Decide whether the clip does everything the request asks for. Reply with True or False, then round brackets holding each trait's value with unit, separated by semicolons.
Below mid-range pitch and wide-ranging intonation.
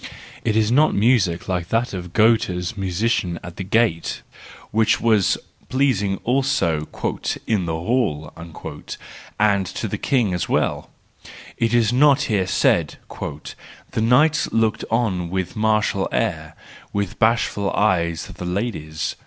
False (105 Hz; 4.6 semitones)